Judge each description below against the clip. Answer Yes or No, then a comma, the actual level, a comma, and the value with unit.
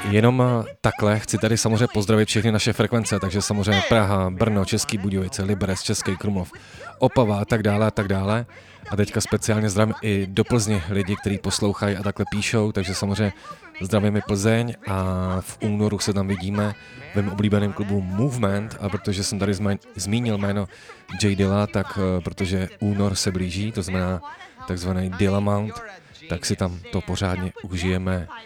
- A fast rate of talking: No, average, 160 wpm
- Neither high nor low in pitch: No, low, 100 Hz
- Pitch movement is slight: Yes, narrow, 1.9 semitones